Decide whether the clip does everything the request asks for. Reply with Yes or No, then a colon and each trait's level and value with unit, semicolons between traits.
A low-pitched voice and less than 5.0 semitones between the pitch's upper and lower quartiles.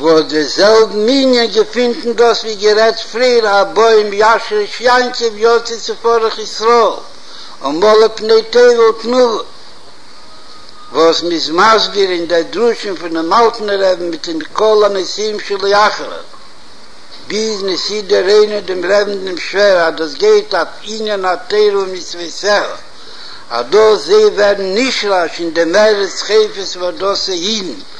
No: high, 210 Hz; average, 3.1 semitones